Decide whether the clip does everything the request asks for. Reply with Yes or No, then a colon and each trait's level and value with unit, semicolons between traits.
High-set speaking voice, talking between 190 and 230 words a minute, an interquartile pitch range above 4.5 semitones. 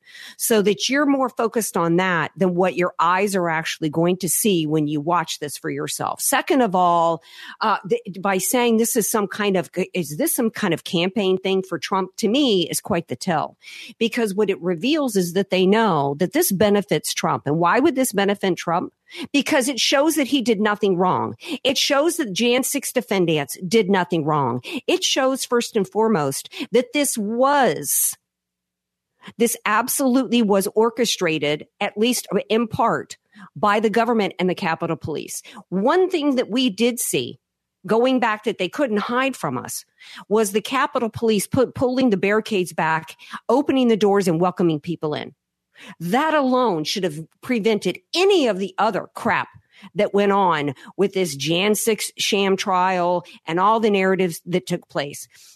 No: high, 205 Hz; average, 175 wpm; average, 5.2 semitones